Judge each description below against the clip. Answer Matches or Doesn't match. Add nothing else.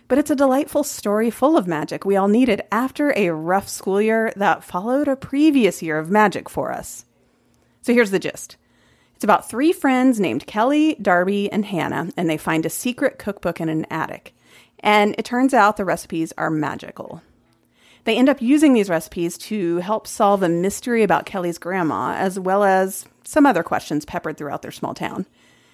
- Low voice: Doesn't match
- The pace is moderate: Matches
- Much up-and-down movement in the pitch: Matches